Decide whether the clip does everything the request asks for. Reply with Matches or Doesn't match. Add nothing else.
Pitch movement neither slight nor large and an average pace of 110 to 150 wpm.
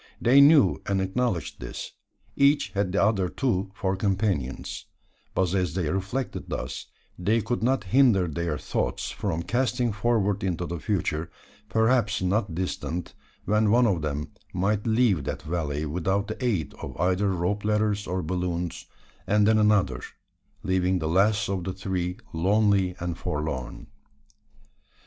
Matches